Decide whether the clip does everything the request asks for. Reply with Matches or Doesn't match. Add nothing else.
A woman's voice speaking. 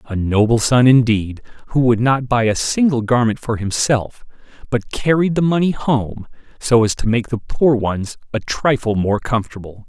Doesn't match